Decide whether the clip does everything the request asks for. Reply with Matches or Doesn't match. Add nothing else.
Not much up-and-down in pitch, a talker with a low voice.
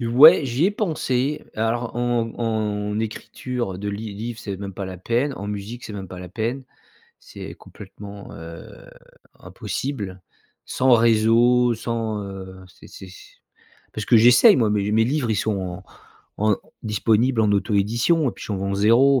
Doesn't match